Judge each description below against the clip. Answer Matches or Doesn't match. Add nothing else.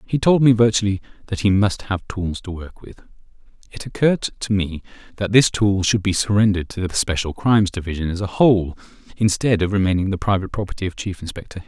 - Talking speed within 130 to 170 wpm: Doesn't match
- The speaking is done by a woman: Doesn't match